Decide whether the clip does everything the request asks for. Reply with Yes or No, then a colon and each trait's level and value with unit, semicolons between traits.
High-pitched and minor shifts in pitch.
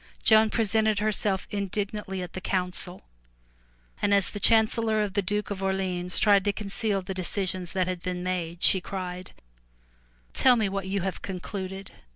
Yes: high, 195 Hz; narrow, 2.1 semitones